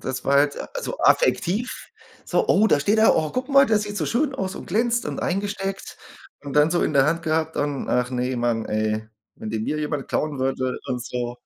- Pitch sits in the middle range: Yes, medium, 150 Hz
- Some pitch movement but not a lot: No, wide, 8.1 semitones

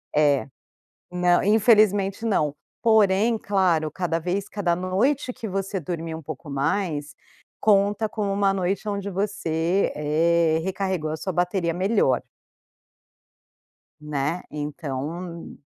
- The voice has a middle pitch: Yes, medium, 180 Hz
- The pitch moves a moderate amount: Yes, average, 3.9 semitones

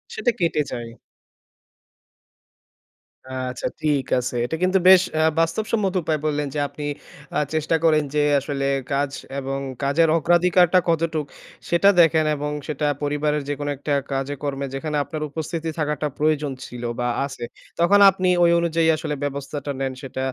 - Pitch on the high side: No, medium, 150 Hz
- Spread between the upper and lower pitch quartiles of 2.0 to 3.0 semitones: Yes, average, 2.7 semitones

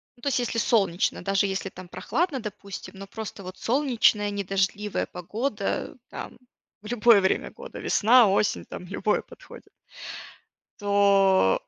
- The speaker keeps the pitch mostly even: No, average, 3.1 semitones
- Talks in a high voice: Yes, high, 205 Hz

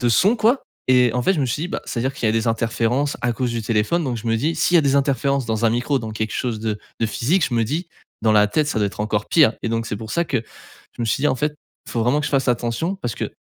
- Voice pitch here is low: Yes, low, 120 Hz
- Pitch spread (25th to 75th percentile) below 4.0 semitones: No, average, 4.3 semitones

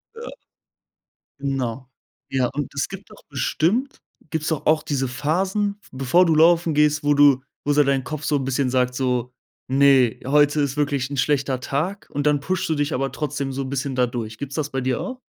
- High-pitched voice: No, medium, 140 Hz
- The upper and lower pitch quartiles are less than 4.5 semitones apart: Yes, average, 2.8 semitones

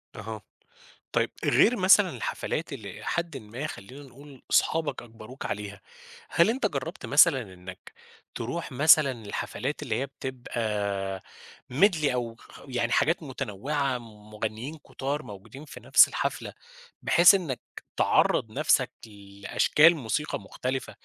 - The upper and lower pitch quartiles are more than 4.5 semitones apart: Yes, wide, 5.5 semitones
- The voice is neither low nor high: No, low, 130 Hz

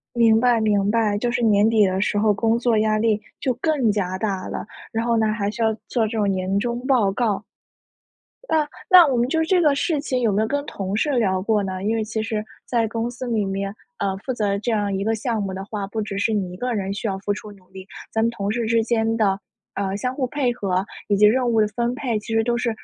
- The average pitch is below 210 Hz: No, high, 220 Hz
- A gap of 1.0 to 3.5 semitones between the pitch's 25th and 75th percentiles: Yes, average, 2.9 semitones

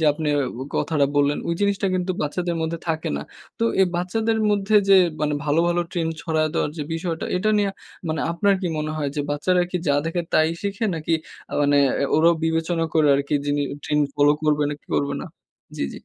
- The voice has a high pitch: No, medium, 160 Hz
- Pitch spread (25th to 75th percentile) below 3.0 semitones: No, average, 3.4 semitones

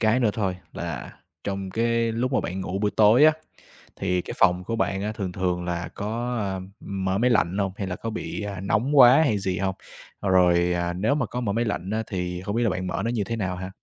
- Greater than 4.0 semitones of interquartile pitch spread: No, average, 3.7 semitones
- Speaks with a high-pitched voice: No, low, 100 Hz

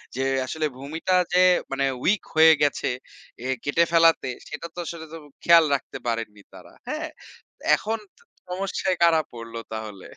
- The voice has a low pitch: No, medium, 160 Hz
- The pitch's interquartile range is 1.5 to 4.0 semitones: No, average, 4.7 semitones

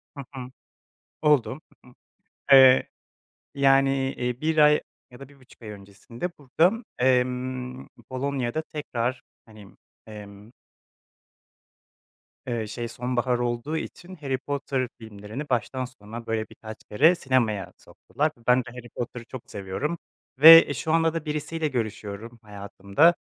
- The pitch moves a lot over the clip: No, average, 3.8 semitones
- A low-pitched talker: Yes, low, 125 Hz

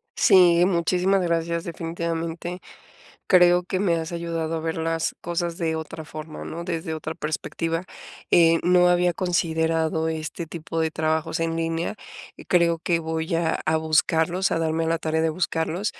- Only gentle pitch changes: Yes, narrow, 1.2 semitones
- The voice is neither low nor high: Yes, medium, 165 Hz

